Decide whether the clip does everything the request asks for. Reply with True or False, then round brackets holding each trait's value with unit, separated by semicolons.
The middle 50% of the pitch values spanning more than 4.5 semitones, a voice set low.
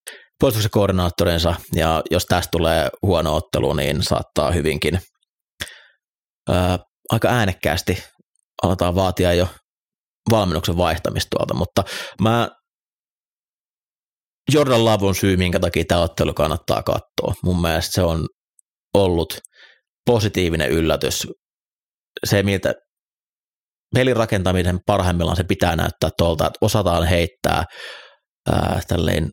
False (3.3 semitones; 90 Hz)